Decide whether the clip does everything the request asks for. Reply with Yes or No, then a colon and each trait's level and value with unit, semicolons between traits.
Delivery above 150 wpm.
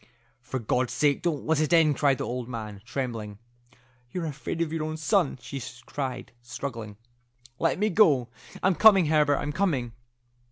Yes: average, 165 wpm